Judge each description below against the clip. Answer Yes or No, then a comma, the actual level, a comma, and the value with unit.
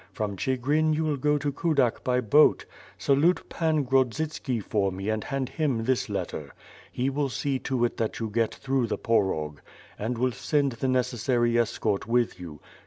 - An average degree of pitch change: Yes, average, 4.0 semitones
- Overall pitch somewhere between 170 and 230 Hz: No, low, 125 Hz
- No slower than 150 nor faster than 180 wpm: Yes, average, 175 wpm